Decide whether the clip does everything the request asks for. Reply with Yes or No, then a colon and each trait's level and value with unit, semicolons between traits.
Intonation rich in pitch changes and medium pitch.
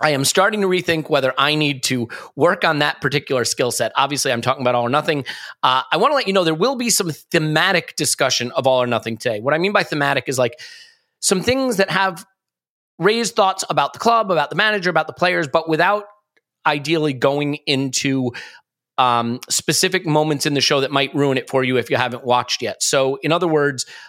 Yes: wide, 5.9 semitones; medium, 155 Hz